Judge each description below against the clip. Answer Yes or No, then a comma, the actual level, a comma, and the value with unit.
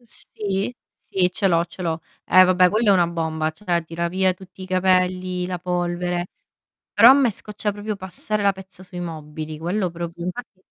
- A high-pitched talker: No, medium, 180 Hz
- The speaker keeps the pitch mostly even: Yes, narrow, 2.0 semitones